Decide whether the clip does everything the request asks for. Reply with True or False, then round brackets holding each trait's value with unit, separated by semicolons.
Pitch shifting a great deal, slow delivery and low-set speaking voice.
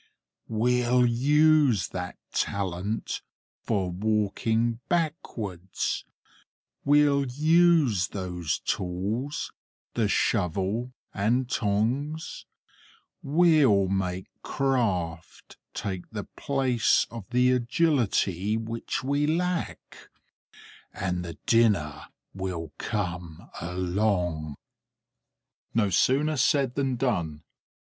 True (6.5 semitones; 80 wpm; 110 Hz)